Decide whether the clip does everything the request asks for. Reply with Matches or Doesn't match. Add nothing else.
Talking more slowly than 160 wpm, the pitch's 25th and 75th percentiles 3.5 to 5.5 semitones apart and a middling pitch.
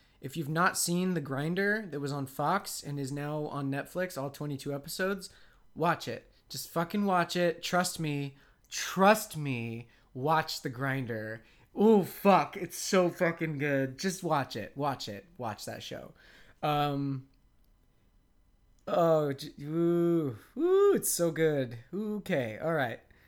Matches